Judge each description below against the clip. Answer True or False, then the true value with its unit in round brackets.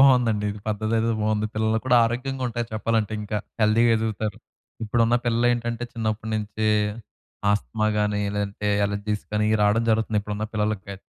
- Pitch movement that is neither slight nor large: False (1.6 semitones)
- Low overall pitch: True (110 Hz)